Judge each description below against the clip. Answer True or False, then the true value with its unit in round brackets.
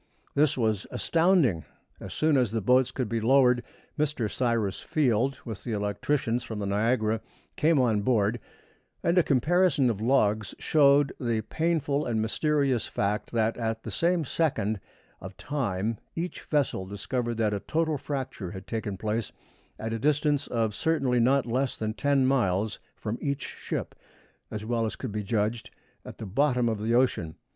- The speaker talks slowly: False (165 wpm)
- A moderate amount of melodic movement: True (4.4 semitones)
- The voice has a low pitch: True (120 Hz)